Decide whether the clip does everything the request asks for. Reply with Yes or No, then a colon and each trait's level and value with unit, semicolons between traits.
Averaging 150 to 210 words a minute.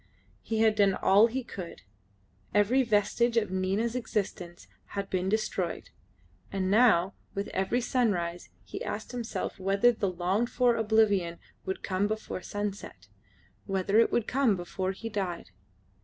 No: average, 140 wpm